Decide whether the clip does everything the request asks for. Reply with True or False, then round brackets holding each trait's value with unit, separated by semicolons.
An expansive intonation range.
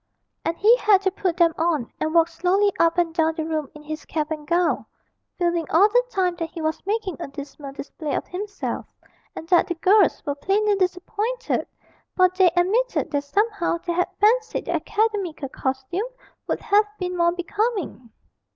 False (4.1 semitones)